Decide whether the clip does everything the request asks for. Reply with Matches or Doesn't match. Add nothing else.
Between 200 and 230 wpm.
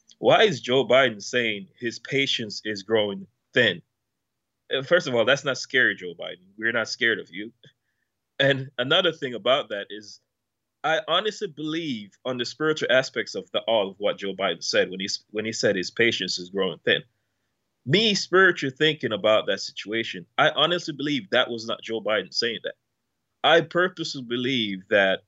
Doesn't match